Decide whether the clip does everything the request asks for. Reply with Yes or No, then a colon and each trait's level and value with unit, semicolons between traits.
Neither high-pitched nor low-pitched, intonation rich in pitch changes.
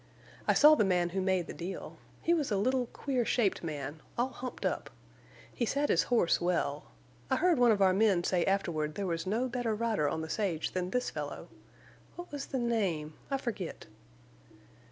No: high, 200 Hz; wide, 6.1 semitones